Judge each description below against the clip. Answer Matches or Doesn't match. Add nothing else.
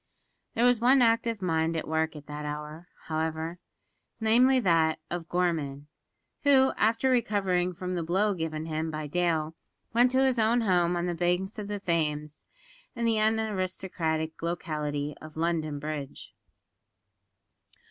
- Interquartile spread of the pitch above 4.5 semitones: Matches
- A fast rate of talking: Doesn't match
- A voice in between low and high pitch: Matches